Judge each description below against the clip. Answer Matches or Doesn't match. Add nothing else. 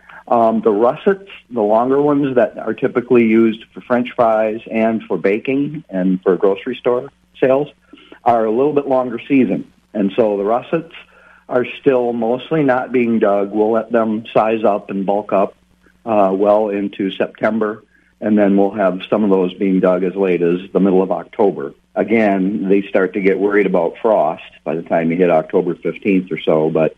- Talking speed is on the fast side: Doesn't match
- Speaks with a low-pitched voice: Matches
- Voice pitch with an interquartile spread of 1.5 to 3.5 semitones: Doesn't match